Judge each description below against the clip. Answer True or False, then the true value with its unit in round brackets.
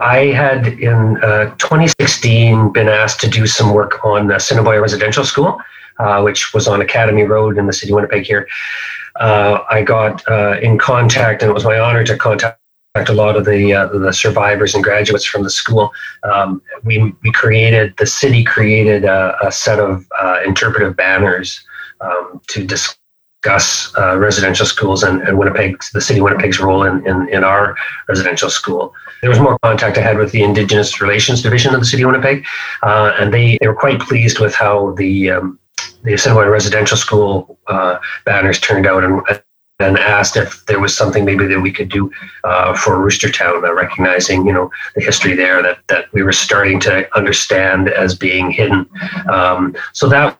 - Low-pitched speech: True (105 Hz)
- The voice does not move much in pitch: True (2.1 semitones)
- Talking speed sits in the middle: True (190 wpm)